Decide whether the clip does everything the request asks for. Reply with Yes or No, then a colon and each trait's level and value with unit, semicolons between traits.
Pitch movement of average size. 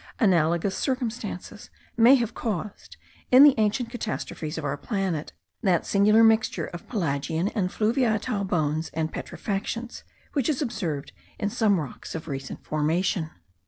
No: wide, 5.9 semitones